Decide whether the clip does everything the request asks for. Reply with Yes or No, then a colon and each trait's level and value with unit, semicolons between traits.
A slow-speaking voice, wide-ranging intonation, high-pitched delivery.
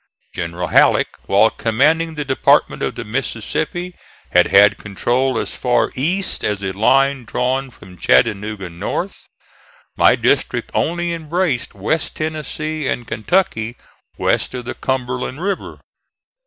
No: slow, 130 wpm; wide, 6.5 semitones; low, 130 Hz